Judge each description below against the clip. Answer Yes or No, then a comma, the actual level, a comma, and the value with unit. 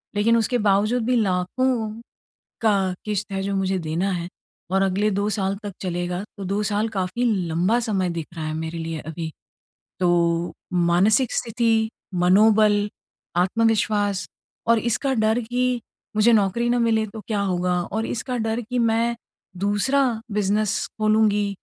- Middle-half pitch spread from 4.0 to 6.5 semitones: No, average, 3.3 semitones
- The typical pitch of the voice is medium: No, high, 210 Hz